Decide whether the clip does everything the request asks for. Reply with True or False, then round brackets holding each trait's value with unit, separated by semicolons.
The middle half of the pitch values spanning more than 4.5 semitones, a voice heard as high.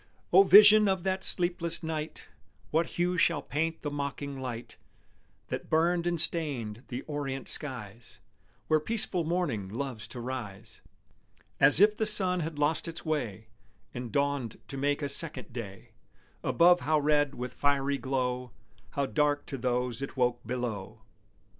False (4.9 semitones; 145 Hz)